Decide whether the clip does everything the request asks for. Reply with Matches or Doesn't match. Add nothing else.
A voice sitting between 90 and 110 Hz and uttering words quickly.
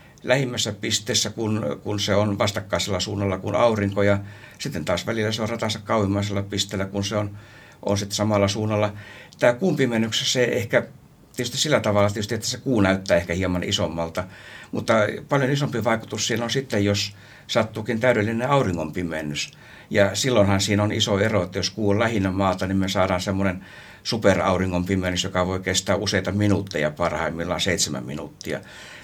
Matches